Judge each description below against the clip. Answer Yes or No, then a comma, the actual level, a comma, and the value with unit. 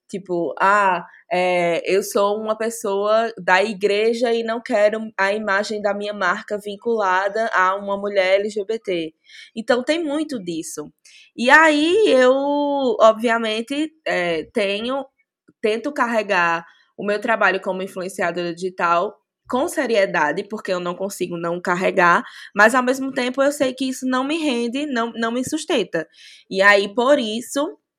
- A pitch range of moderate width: Yes, average, 5.0 semitones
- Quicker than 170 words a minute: No, average, 145 wpm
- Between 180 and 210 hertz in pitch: No, high, 220 Hz